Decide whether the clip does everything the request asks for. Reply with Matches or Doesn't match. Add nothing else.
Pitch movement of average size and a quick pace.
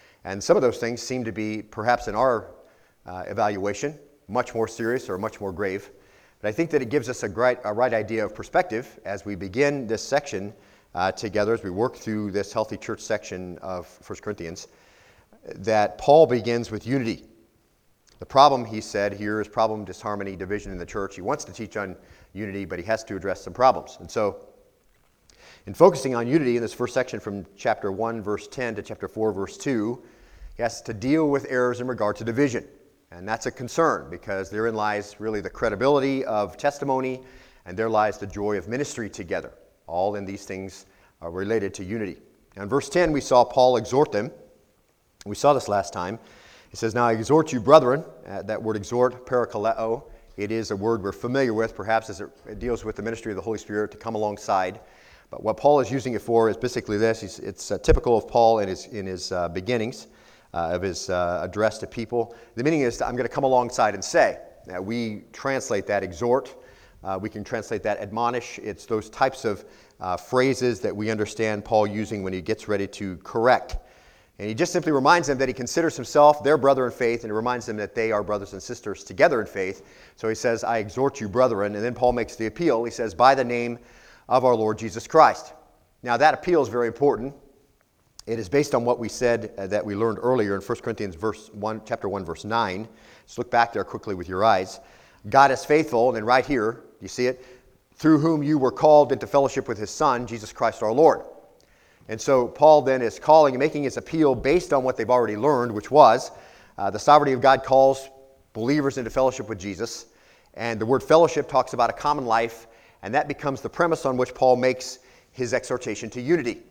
Matches